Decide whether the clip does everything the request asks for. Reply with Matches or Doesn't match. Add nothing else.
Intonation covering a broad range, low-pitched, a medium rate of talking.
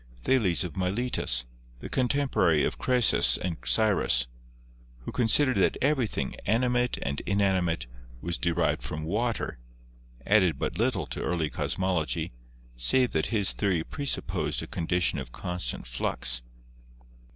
Doesn't match